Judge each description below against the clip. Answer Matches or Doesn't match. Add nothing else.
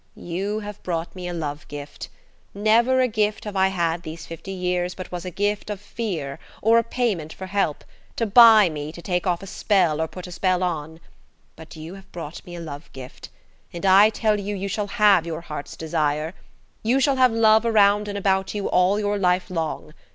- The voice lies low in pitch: Doesn't match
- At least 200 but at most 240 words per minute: Matches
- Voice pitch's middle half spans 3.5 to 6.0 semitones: Matches